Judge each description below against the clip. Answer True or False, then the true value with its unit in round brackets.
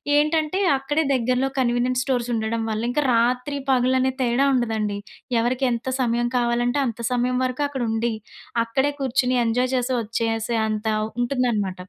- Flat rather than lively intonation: True (2.1 semitones)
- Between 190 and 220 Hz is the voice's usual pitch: False (245 Hz)